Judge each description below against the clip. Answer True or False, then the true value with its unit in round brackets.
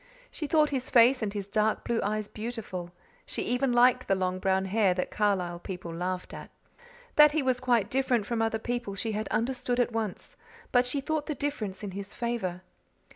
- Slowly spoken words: False (195 wpm)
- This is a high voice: True (225 Hz)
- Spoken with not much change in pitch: False (4.4 semitones)